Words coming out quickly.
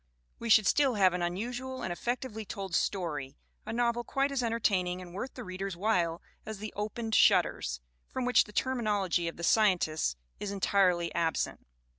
No: average, 180 wpm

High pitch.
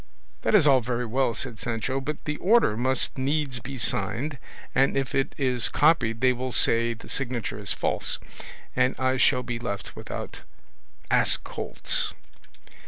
No: low, 130 Hz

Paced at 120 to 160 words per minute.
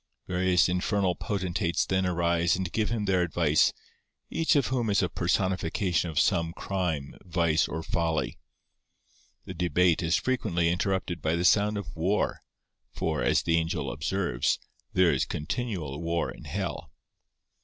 Yes: average, 145 wpm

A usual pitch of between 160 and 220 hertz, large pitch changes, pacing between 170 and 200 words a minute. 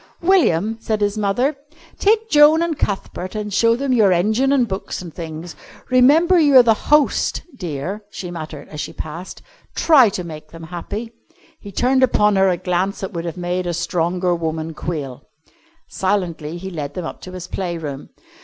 Yes: high, 190 Hz; wide, 5.8 semitones; average, 180 wpm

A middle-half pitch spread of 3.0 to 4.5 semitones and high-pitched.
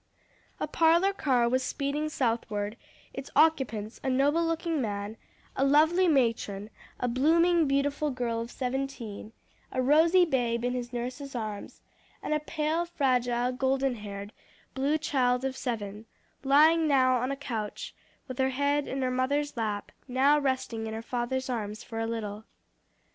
Yes: average, 3.9 semitones; very high, 260 Hz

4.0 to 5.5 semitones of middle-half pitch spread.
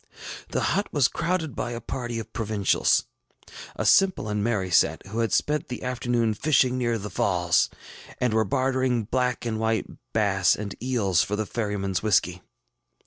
No: average, 3.6 semitones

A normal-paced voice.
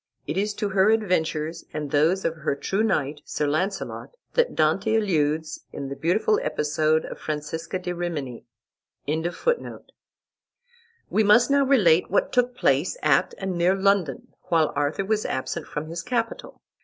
Yes: average, 150 wpm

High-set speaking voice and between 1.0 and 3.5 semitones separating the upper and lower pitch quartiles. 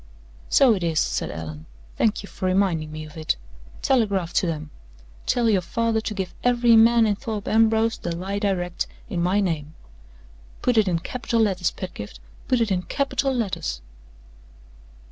No: high, 195 Hz; average, 5.1 semitones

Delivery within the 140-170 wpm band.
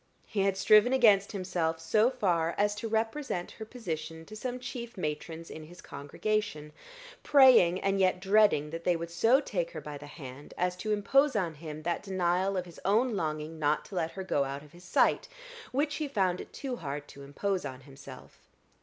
No: average, 200 wpm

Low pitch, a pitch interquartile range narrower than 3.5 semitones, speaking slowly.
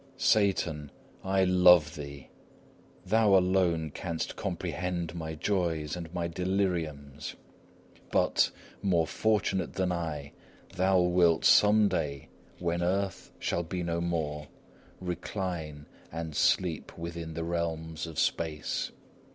Yes: very low, 85 Hz; narrow, 2.4 semitones; slow, 110 wpm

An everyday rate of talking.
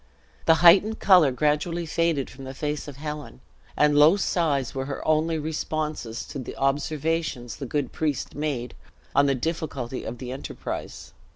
Yes: average, 160 wpm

